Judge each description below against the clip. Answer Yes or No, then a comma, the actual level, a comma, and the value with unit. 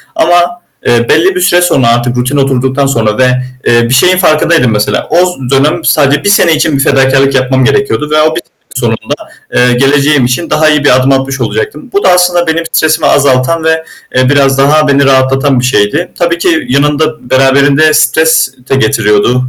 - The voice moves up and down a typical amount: Yes, average, 3.4 semitones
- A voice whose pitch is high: No, medium, 140 Hz